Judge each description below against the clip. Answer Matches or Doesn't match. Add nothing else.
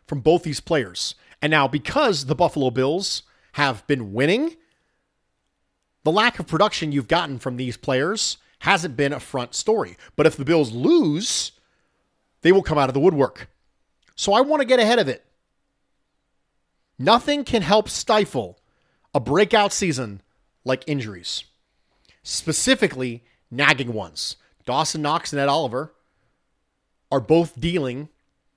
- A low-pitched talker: Doesn't match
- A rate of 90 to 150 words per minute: Matches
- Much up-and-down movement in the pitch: Matches